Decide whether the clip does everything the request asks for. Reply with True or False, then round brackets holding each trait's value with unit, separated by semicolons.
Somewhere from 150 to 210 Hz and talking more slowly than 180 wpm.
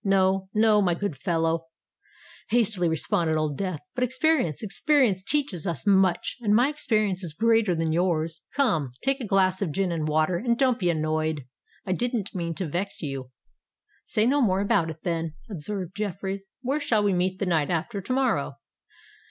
True (190 Hz; 170 wpm)